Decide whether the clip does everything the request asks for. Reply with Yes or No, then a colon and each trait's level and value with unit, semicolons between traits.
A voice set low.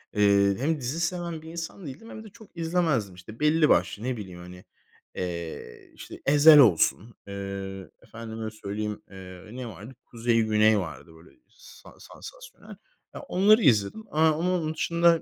Yes: low, 115 Hz